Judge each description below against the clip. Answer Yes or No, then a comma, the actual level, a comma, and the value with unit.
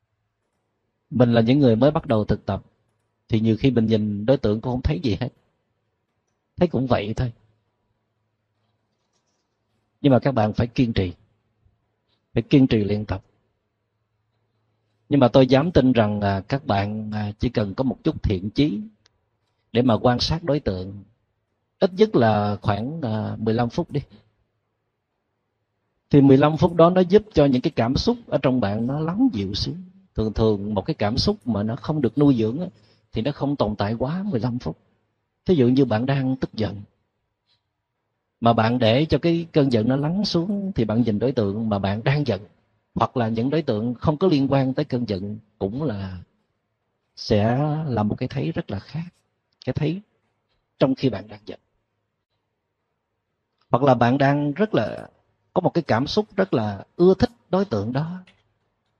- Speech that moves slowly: No, average, 180 wpm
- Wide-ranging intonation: No, average, 4.3 semitones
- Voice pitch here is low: Yes, low, 115 Hz